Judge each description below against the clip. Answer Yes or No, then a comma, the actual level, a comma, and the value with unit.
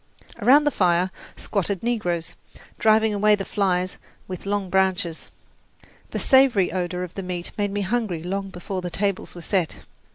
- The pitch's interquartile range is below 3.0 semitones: Yes, narrow, 2.6 semitones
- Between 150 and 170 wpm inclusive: Yes, average, 160 wpm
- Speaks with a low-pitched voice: No, high, 190 Hz